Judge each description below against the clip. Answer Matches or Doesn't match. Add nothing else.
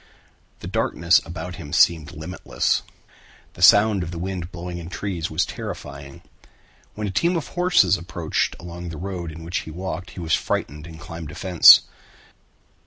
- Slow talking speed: Doesn't match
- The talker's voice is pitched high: Doesn't match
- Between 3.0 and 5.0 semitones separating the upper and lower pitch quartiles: Doesn't match